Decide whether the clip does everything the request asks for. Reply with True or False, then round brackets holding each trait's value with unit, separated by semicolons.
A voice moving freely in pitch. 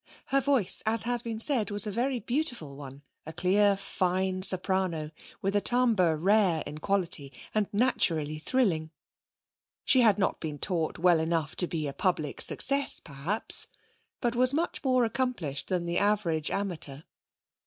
True (6.2 semitones)